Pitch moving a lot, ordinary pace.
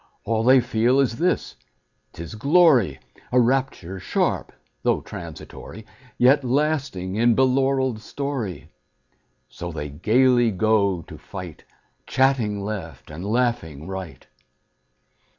No: wide, 6.0 semitones; slow, 115 wpm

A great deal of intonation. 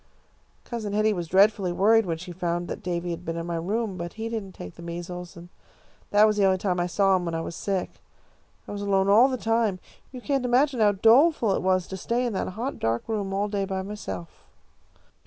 No: average, 3.9 semitones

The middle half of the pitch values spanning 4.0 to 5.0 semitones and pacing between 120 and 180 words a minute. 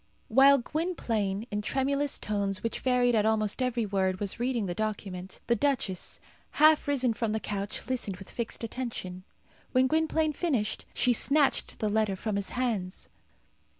Yes: average, 4.4 semitones; average, 155 wpm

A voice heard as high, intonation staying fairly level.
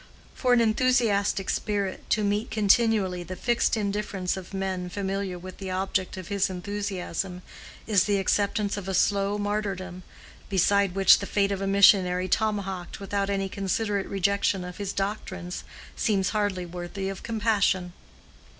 Yes: high, 195 Hz; narrow, 1.7 semitones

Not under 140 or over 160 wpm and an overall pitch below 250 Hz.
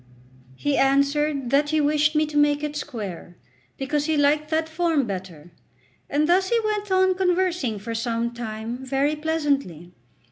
No: average, 155 wpm; very high, 290 Hz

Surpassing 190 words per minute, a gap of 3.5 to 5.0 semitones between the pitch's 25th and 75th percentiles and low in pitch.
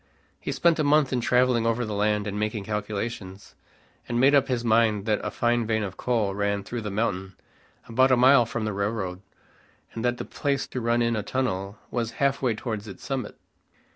No: fast, 205 wpm; average, 3.0 semitones; low, 115 Hz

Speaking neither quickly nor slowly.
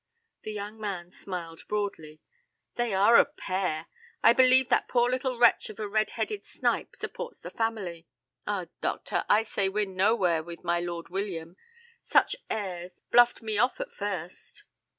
Yes: average, 160 wpm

